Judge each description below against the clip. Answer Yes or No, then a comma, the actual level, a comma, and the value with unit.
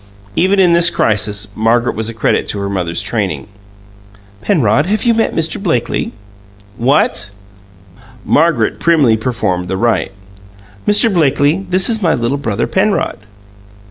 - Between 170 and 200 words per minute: No, average, 140 wpm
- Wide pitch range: Yes, wide, 8.4 semitones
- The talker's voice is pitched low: Yes, low, 130 Hz